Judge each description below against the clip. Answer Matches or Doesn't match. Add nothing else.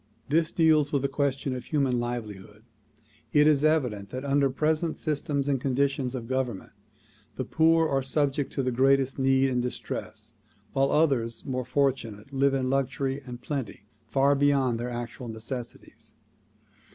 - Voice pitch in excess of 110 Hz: Matches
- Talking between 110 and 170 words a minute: Matches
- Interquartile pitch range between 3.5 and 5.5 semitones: Doesn't match